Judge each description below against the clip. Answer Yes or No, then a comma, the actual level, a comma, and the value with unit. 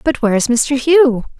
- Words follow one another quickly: Yes, fast, 215 wpm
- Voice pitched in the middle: No, high, 245 Hz